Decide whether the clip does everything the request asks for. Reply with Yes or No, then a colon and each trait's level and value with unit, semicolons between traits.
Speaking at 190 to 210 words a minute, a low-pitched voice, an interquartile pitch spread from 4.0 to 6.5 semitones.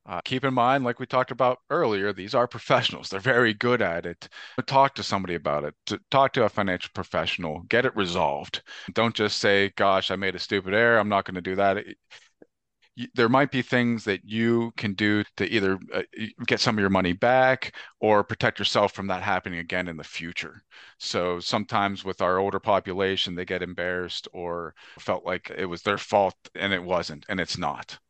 Yes: average, 200 wpm; low, 100 Hz; average, 4.5 semitones